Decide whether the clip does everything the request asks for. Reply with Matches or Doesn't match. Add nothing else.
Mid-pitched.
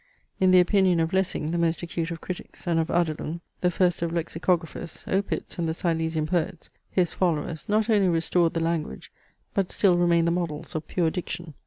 Matches